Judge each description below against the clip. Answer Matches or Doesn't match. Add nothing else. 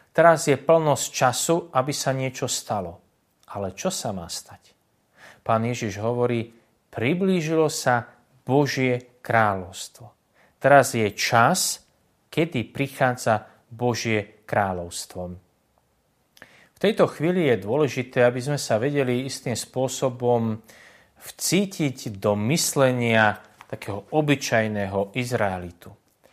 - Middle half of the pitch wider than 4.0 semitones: Matches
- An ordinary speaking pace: Doesn't match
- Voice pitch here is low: Matches